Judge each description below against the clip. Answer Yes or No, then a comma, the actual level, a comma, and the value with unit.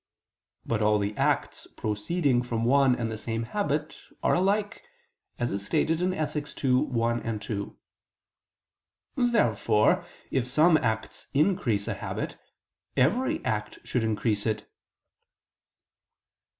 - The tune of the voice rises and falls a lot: Yes, wide, 6.5 semitones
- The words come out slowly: Yes, slow, 105 wpm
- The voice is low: Yes, low, 120 Hz